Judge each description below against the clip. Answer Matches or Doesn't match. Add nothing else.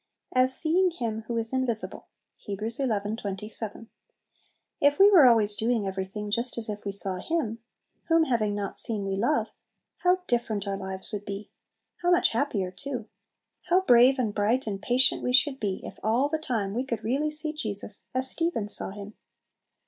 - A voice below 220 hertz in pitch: Doesn't match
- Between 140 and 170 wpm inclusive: Doesn't match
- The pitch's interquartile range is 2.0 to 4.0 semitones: Doesn't match